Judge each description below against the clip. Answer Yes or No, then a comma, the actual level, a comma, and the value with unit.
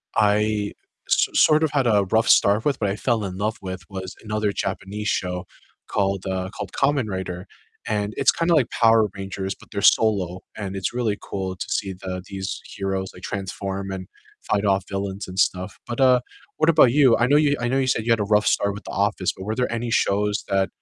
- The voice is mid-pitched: No, low, 100 Hz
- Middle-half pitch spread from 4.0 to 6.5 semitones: No, average, 3.0 semitones